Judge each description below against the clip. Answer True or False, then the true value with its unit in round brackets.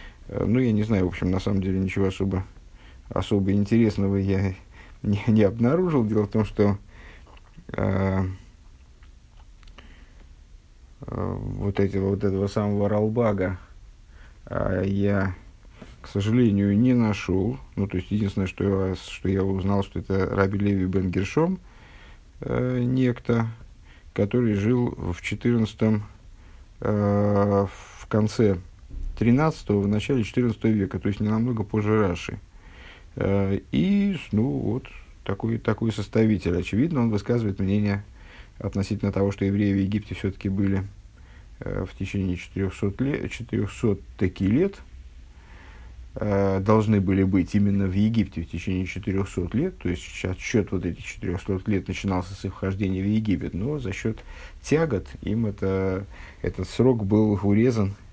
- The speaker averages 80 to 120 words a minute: False (130 wpm)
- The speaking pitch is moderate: False (100 Hz)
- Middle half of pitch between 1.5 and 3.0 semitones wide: True (2.4 semitones)